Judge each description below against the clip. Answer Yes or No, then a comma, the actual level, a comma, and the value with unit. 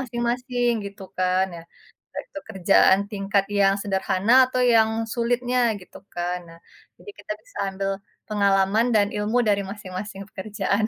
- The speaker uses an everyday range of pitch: Yes, average, 3.3 semitones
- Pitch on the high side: Yes, high, 200 Hz